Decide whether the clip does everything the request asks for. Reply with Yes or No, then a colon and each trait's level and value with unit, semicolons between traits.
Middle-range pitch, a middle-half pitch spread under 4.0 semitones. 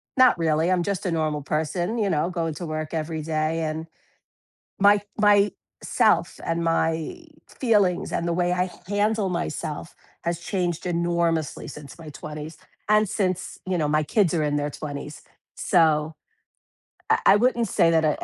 Yes: medium, 170 Hz; average, 3.2 semitones